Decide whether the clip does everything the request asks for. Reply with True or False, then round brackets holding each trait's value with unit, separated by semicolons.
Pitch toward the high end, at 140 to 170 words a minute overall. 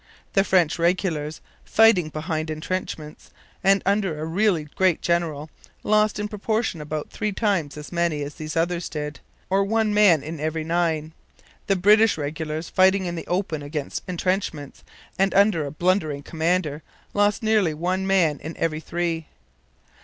False (170 Hz; 155 wpm)